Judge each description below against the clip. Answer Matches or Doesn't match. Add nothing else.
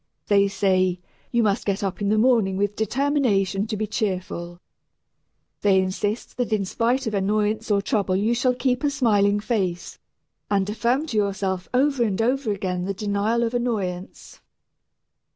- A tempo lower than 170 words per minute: Matches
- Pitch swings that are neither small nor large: Matches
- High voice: Matches